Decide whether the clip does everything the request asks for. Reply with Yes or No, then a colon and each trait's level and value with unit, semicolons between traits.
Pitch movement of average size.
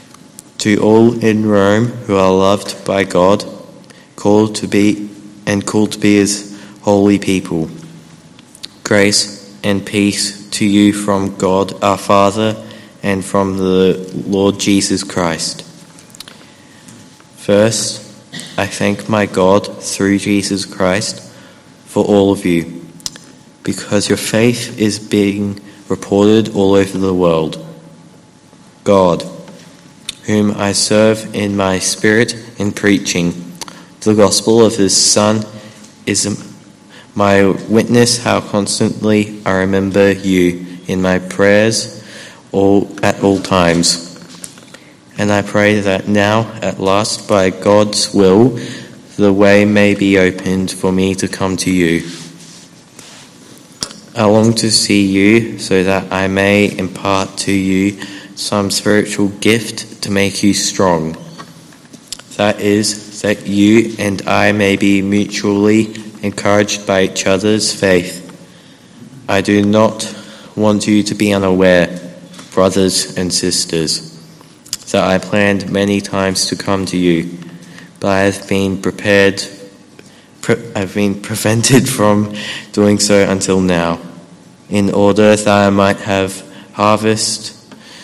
No: narrow, 1.6 semitones